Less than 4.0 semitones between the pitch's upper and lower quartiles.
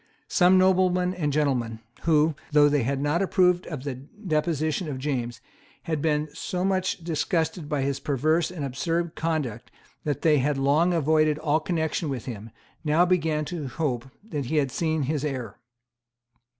Yes: average, 3.3 semitones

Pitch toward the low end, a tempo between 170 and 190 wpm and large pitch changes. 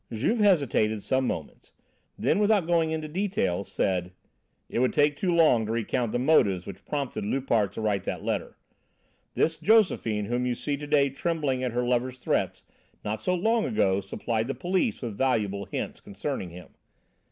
Yes: low, 130 Hz; average, 175 wpm; wide, 6.9 semitones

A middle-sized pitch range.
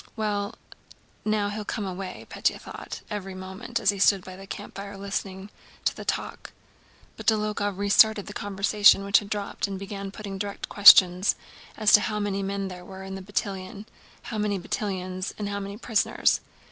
No: narrow, 1.3 semitones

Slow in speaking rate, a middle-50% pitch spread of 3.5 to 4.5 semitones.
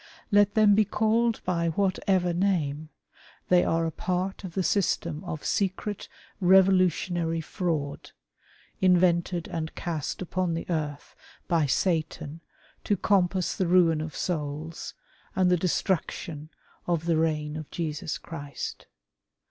No: slow, 125 wpm; average, 2.9 semitones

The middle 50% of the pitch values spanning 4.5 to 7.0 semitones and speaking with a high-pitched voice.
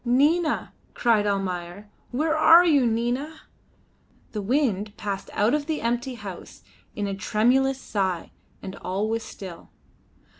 Yes: average, 5.2 semitones; high, 230 Hz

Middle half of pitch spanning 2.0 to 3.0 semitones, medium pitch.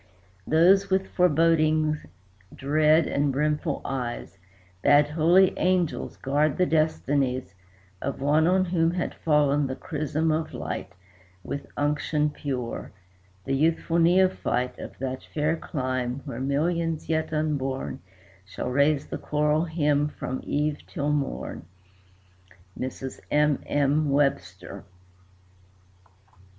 Yes: average, 2.7 semitones; medium, 150 Hz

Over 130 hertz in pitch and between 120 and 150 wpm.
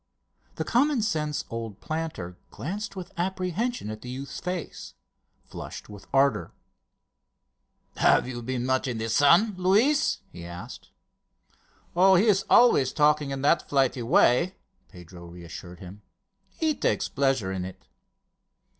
Yes: medium, 140 Hz; slow, 135 wpm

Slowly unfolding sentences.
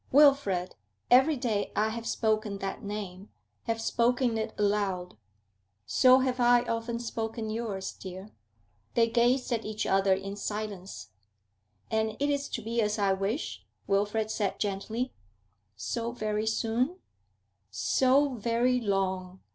Yes: slow, 130 wpm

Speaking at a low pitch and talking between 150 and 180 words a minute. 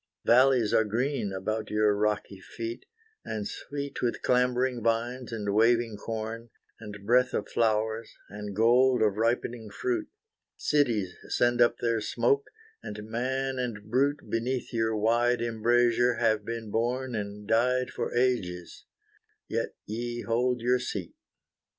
No: low, 115 Hz; slow, 135 wpm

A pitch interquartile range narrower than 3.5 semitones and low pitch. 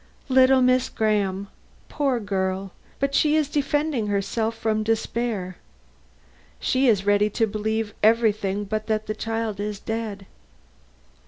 No: average, 2.7 semitones; high, 220 Hz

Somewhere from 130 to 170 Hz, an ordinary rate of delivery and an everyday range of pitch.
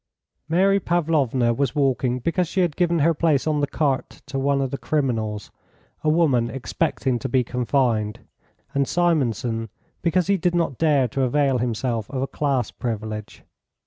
Yes: low, 135 Hz; average, 165 wpm; average, 4.8 semitones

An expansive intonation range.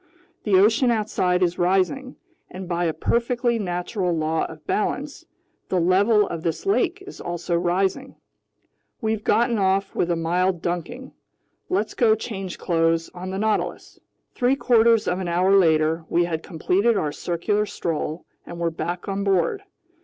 No: average, 4.4 semitones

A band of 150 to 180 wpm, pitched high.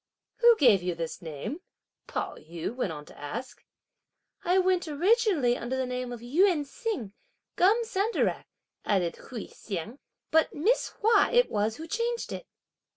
Yes: average, 155 wpm; very high, 275 Hz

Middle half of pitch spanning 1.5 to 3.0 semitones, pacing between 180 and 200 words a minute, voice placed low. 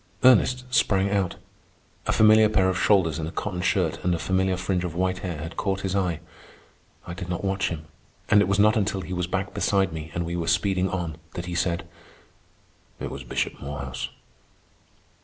Yes: narrow, 2.5 semitones; average, 195 wpm; very low, 90 Hz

